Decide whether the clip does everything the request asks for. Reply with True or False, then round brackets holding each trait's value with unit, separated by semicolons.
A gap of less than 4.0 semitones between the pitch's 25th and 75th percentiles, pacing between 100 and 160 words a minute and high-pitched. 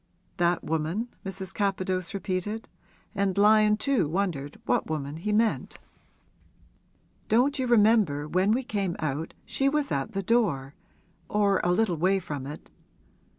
False (4.8 semitones; 140 wpm; 195 Hz)